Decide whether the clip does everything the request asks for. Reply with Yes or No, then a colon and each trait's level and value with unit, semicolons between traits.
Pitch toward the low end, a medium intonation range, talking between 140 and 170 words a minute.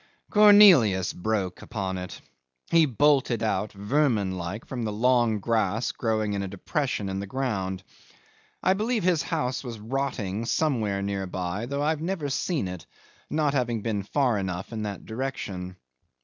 No: low, 110 Hz; wide, 5.9 semitones; average, 155 wpm